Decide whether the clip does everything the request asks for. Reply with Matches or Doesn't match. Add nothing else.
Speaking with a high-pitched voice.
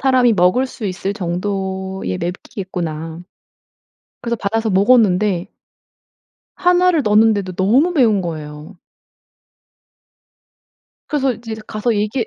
Matches